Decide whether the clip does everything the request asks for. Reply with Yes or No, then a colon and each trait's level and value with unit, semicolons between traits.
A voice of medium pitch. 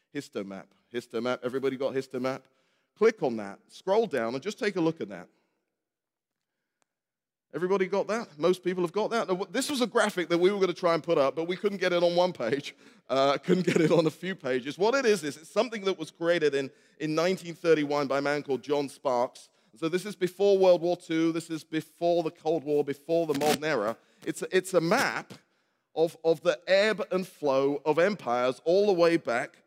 Yes: medium, 165 Hz